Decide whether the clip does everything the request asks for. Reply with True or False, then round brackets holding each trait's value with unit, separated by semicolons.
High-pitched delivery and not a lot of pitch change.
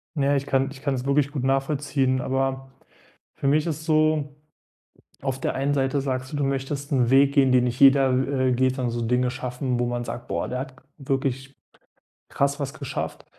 False (135 Hz; 1.5 semitones)